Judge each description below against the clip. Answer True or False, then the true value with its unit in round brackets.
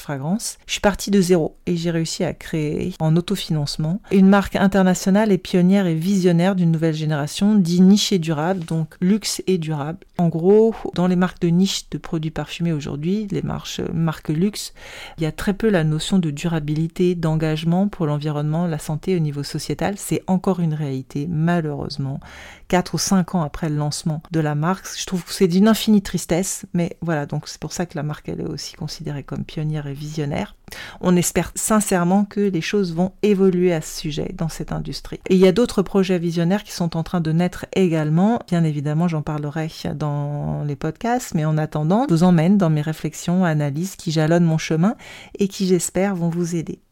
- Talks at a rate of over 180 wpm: True (200 wpm)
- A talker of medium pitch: True (170 Hz)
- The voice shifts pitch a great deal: False (3.3 semitones)